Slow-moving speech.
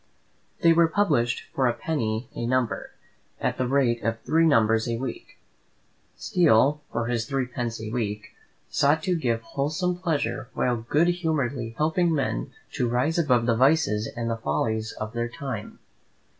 No: average, 155 wpm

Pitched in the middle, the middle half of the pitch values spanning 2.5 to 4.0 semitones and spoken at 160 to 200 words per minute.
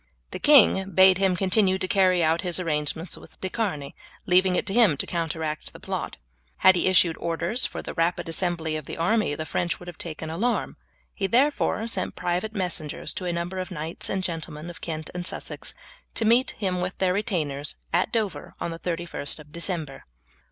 Yes: medium, 180 Hz; average, 2.8 semitones; average, 195 wpm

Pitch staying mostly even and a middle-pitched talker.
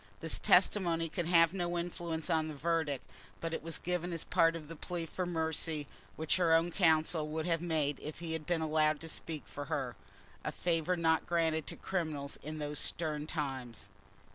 Yes: narrow, 1.8 semitones; medium, 160 Hz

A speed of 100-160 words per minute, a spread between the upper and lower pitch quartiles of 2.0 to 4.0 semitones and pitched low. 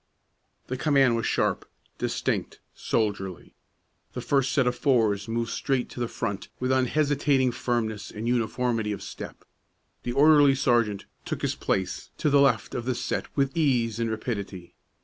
Yes: average, 155 wpm; average, 3.5 semitones; low, 120 Hz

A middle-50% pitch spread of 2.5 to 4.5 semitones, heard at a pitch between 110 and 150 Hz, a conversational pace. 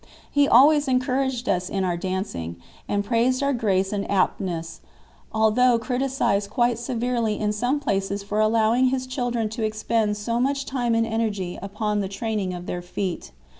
No: average, 3.9 semitones; high, 220 Hz; average, 165 wpm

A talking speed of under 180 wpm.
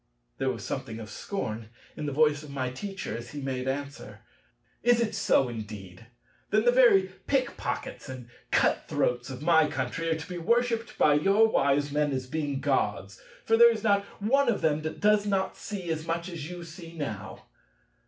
No: average, 195 wpm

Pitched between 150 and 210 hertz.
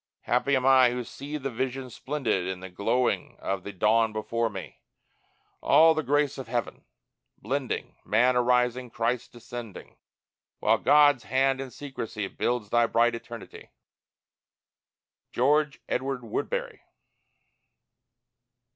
No: low, 125 Hz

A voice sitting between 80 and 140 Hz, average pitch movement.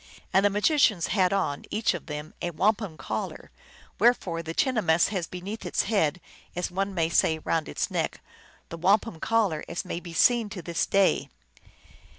No: medium, 180 Hz; average, 3.9 semitones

